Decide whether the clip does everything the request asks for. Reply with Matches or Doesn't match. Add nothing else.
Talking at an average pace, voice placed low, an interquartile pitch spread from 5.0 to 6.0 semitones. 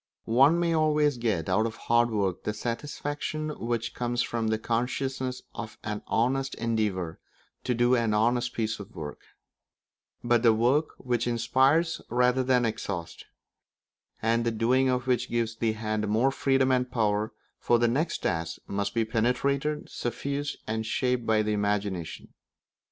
Doesn't match